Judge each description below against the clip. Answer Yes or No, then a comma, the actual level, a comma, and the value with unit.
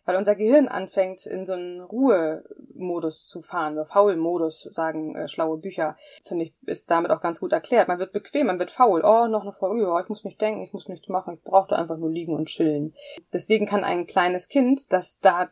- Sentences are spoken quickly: Yes, fast, 215 wpm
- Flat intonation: No, average, 3.6 semitones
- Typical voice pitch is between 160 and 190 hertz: Yes, medium, 185 Hz